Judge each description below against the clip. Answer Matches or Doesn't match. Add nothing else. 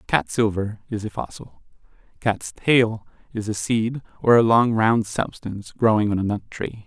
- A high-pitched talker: Doesn't match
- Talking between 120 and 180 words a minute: Matches